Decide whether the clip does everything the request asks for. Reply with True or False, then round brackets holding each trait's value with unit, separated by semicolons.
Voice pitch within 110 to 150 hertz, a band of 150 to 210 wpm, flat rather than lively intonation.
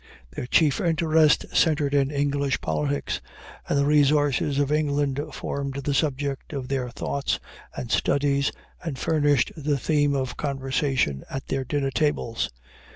False (140 Hz; 140 wpm; 1.6 semitones)